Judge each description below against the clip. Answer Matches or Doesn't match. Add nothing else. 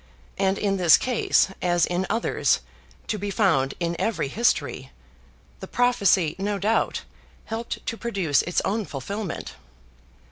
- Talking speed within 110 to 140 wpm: Matches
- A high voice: Matches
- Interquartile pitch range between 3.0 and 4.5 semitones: Matches